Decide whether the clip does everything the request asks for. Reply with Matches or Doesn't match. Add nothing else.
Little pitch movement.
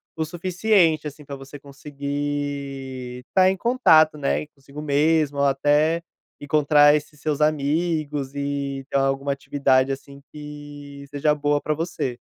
Matches